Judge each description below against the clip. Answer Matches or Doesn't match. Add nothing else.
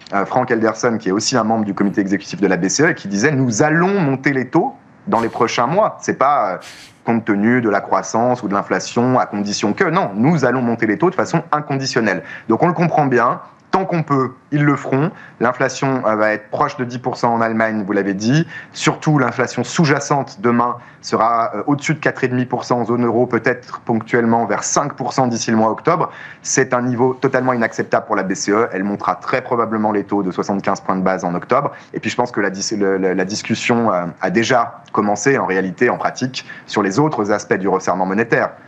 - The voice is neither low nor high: Doesn't match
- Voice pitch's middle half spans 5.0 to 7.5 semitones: Doesn't match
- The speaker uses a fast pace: Doesn't match